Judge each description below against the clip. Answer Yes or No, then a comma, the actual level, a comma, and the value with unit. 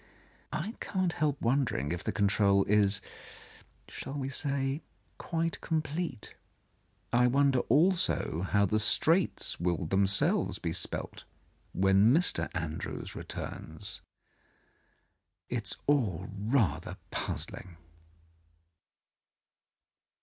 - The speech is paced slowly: Yes, slow, 110 wpm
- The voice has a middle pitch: No, low, 120 Hz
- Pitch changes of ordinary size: No, wide, 6.8 semitones